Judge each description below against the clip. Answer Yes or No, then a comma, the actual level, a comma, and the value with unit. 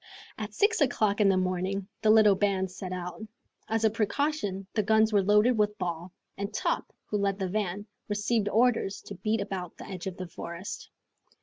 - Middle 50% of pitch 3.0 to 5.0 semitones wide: No, narrow, 2.5 semitones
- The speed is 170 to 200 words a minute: Yes, average, 190 wpm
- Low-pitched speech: No, high, 200 Hz